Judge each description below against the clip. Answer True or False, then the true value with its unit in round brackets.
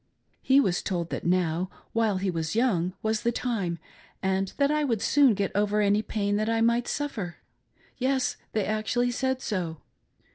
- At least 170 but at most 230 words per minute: True (175 wpm)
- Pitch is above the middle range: True (210 Hz)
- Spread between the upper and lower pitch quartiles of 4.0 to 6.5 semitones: True (4.6 semitones)